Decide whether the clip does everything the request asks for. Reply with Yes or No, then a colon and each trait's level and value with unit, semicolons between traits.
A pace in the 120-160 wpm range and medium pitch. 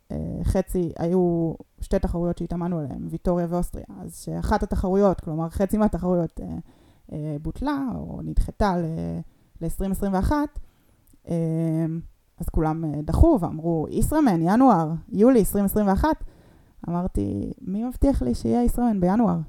No: slow, 100 wpm; medium, 175 Hz